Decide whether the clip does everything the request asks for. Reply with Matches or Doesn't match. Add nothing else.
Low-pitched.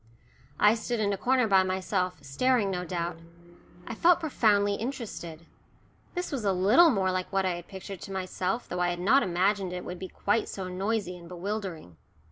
Doesn't match